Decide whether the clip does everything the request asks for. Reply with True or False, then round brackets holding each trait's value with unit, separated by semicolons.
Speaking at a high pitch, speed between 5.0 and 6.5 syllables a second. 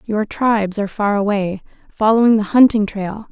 True (210 Hz; 5.1 syllables/s)